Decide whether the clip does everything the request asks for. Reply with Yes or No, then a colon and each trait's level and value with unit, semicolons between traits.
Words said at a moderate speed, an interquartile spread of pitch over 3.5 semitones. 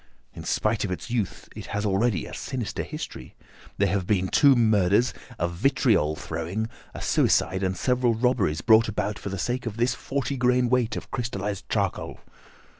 Yes: average, 175 wpm; average, 4.3 semitones